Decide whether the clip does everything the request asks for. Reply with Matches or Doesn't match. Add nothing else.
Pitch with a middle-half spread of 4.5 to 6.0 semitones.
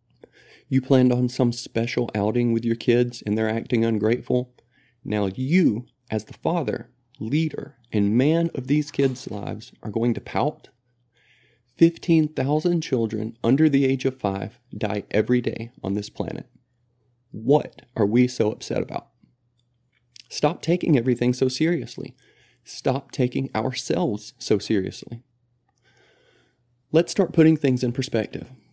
Doesn't match